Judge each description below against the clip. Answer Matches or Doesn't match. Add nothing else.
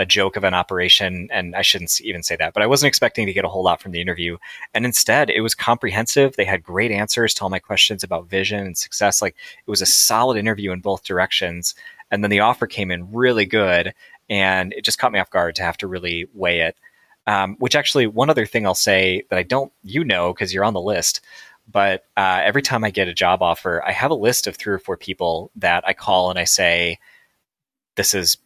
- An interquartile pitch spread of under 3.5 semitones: Doesn't match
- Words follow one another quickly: Matches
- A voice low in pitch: Matches